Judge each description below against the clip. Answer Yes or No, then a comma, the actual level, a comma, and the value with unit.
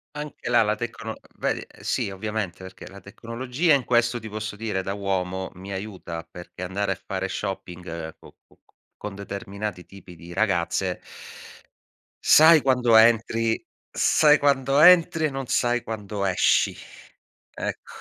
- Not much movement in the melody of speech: No, average, 4.3 semitones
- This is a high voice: No, low, 105 Hz